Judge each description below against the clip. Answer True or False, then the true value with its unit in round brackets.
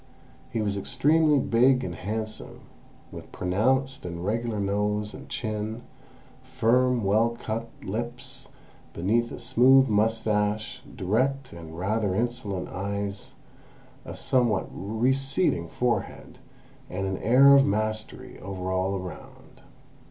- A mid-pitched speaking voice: False (110 Hz)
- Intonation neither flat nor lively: True (4.1 semitones)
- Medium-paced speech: False (115 wpm)